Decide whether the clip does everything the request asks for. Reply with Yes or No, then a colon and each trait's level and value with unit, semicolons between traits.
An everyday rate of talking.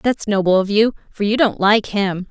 No: fast, 210 wpm